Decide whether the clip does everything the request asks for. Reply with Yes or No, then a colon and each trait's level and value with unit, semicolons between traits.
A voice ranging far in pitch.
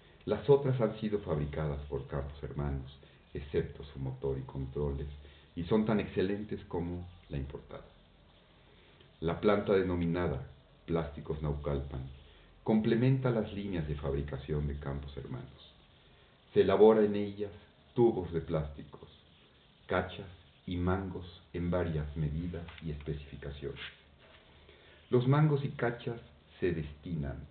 Yes: wide, 5.9 semitones